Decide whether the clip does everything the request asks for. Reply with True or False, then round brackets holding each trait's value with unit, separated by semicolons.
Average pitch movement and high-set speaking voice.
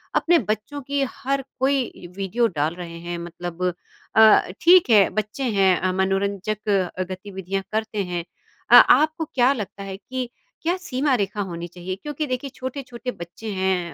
False (5.8 semitones; 210 Hz)